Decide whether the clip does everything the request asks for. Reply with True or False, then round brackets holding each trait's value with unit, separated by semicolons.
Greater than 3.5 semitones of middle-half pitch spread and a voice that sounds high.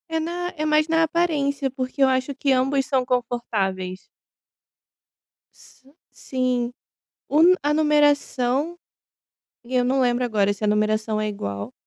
True (4.4 semitones; 260 Hz)